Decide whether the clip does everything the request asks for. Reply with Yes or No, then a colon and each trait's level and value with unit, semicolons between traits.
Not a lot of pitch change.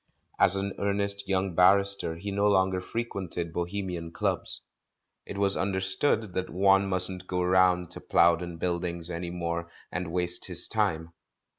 Yes: narrow, 2.1 semitones